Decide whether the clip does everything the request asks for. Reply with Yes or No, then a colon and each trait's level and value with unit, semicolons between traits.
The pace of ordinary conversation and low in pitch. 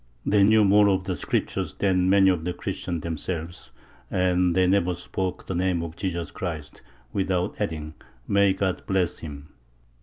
Yes: average, 160 wpm; very low, 90 Hz